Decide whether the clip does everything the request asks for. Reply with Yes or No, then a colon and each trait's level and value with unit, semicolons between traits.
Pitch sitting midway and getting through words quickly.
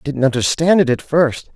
Yes: medium, 145 Hz; fast, 230 wpm